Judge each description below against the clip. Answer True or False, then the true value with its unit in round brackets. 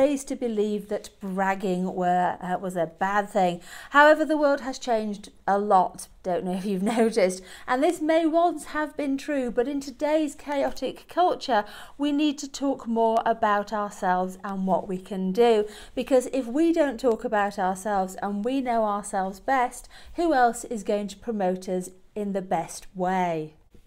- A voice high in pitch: True (215 Hz)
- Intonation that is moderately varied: False (6.0 semitones)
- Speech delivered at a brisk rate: False (175 wpm)